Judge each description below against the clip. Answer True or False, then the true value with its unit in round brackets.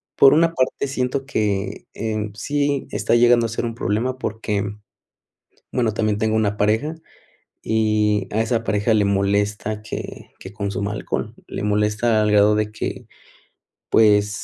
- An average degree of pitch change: False (2.3 semitones)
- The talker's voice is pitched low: True (110 Hz)